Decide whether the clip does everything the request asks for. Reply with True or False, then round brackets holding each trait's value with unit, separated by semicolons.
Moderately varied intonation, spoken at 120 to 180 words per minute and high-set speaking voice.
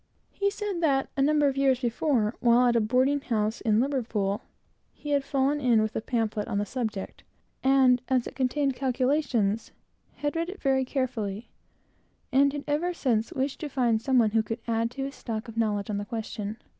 False (3.8 semitones; 195 wpm; 255 Hz)